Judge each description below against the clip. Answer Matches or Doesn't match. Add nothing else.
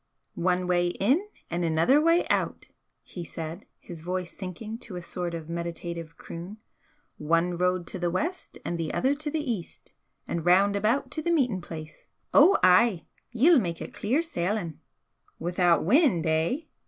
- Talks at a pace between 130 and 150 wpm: Doesn't match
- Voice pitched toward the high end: Doesn't match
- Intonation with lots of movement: Matches